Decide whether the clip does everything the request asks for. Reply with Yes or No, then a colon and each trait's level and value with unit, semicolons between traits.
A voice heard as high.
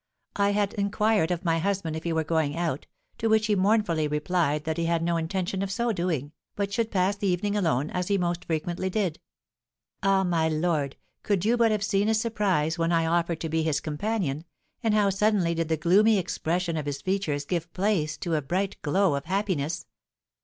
No: medium, 175 Hz